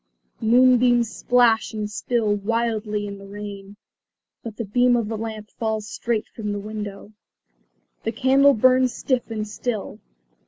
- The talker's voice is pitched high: Yes, high, 220 Hz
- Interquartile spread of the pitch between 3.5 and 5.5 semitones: No, narrow, 2.5 semitones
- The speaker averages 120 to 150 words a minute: Yes, average, 145 wpm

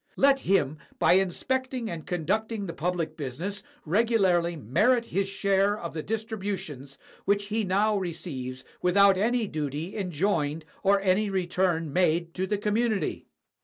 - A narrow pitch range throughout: No, average, 4.0 semitones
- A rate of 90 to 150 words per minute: Yes, average, 140 wpm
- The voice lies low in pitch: No, high, 190 Hz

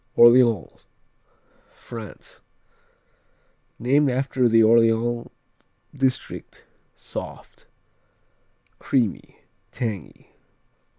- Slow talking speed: Yes, slow, 55 wpm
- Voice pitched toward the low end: Yes, low, 120 Hz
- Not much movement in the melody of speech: Yes, narrow, 2.2 semitones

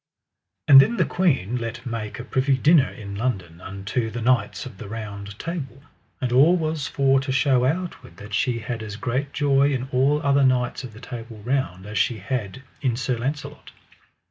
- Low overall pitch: Yes, low, 125 Hz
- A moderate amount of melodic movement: Yes, average, 4.0 semitones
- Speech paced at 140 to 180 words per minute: No, average, 190 wpm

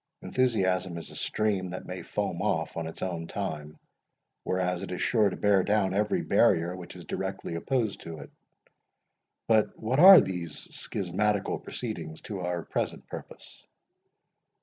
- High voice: No, very low, 95 Hz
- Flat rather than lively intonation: No, average, 3.6 semitones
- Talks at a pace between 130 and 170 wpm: Yes, average, 150 wpm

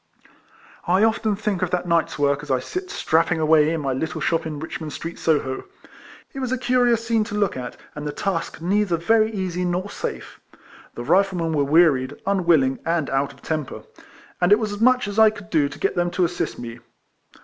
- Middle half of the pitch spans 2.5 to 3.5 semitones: No, wide, 5.5 semitones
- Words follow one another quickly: Yes, fast, 215 wpm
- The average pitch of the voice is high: No, medium, 175 Hz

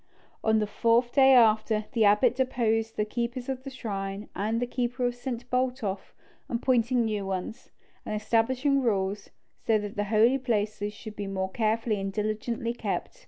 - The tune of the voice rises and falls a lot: No, average, 2.8 semitones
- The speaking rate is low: No, average, 165 wpm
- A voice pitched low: No, high, 225 Hz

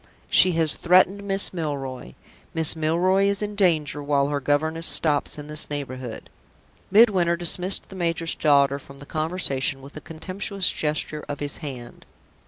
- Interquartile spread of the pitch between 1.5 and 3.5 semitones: No, average, 4.1 semitones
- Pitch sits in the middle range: Yes, medium, 155 Hz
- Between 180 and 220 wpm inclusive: No, average, 155 wpm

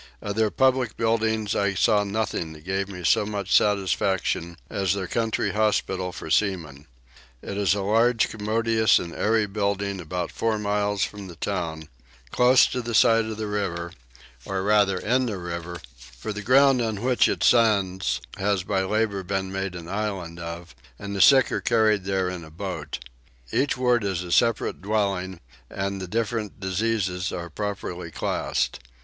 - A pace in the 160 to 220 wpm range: Yes, average, 170 wpm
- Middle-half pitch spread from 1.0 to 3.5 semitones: Yes, average, 3.2 semitones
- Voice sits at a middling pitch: No, low, 100 Hz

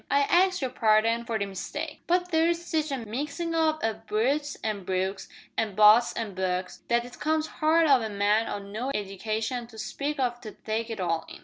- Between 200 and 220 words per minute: Yes, fast, 205 wpm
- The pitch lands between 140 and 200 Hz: No, high, 230 Hz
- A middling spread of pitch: No, wide, 6.0 semitones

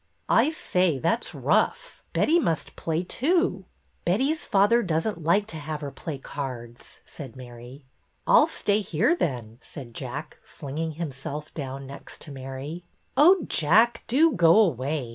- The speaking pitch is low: No, medium, 160 Hz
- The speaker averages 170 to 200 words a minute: Yes, average, 175 wpm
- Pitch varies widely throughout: Yes, wide, 7.4 semitones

